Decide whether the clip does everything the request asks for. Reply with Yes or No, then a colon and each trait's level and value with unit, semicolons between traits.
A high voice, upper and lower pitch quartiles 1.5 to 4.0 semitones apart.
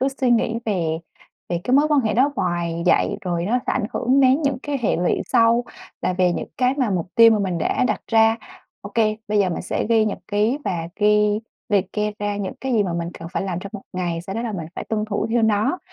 No: high, 210 Hz; average, 4.4 semitones